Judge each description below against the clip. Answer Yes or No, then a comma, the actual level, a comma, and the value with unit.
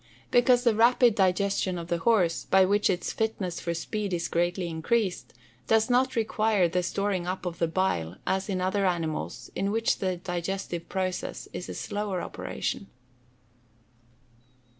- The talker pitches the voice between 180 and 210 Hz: Yes, high, 190 Hz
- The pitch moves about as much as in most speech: Yes, average, 3.3 semitones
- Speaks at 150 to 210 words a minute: Yes, average, 160 wpm